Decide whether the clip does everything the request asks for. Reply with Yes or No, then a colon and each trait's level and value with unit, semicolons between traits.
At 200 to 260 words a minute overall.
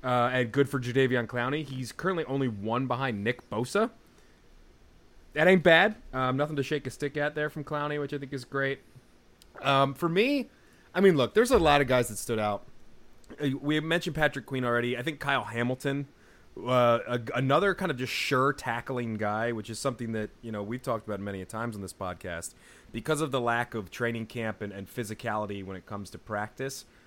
Yes: fast, 205 wpm